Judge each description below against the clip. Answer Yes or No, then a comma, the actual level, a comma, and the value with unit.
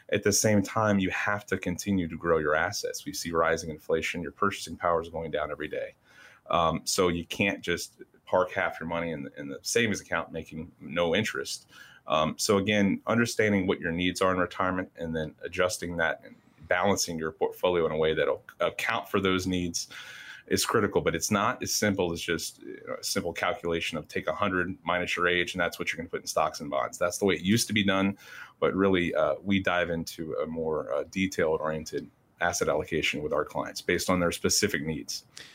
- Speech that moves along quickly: Yes, fast, 210 wpm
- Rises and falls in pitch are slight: No, average, 3.2 semitones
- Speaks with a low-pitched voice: Yes, very low, 95 Hz